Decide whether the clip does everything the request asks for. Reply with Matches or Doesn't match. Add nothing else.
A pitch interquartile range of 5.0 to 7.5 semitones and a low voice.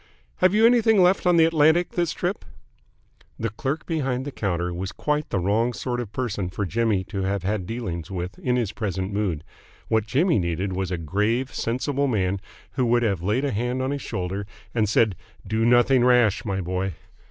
Matches